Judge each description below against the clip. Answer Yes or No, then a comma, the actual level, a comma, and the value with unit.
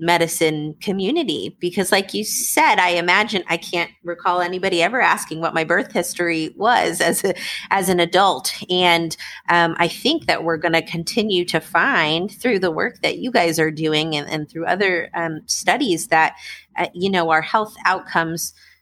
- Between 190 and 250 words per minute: No, average, 175 wpm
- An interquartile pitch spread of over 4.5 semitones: No, average, 2.7 semitones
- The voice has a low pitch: No, medium, 175 Hz